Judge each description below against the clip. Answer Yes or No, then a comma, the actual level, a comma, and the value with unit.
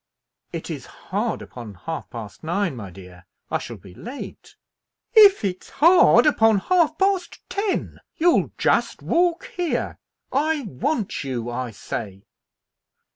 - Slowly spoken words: Yes, slow, 130 wpm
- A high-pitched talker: Yes, high, 205 Hz